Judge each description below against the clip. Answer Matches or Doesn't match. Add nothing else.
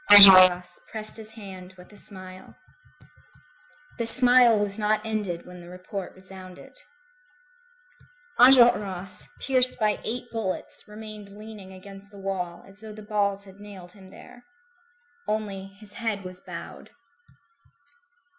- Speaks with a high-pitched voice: Matches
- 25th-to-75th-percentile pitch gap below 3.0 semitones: Matches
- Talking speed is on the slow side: Matches